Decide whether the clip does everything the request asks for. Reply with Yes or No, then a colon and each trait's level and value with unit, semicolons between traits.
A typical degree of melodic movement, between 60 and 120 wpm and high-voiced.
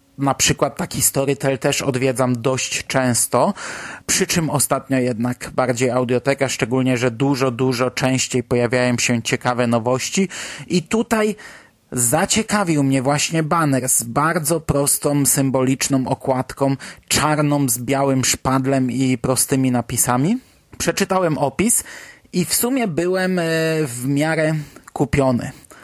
No: average, 3.3 semitones; average, 115 wpm; low, 135 Hz